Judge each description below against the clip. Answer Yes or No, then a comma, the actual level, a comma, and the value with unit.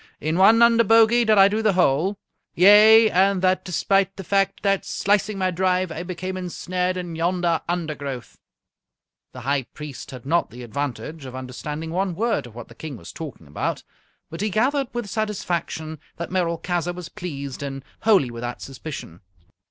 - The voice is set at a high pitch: No, medium, 175 Hz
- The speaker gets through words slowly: No, average, 170 wpm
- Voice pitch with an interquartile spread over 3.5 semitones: Yes, wide, 5.5 semitones